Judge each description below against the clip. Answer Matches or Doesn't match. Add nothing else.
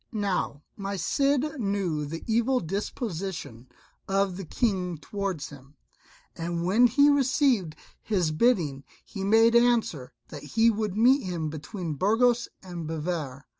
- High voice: Matches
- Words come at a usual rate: Doesn't match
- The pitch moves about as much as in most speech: Doesn't match